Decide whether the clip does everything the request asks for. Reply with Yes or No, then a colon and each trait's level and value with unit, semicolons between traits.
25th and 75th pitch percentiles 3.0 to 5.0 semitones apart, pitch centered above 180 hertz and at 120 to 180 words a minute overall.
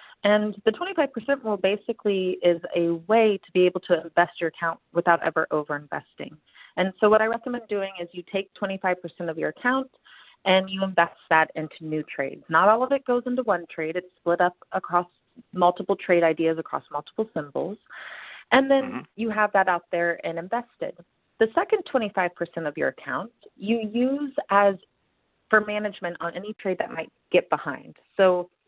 Yes: average, 4.3 semitones; high, 190 Hz; average, 175 wpm